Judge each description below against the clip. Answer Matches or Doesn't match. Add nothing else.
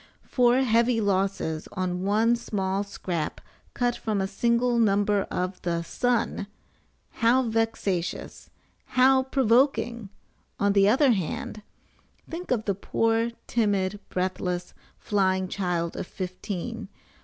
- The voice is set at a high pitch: Matches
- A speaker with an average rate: Doesn't match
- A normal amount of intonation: Matches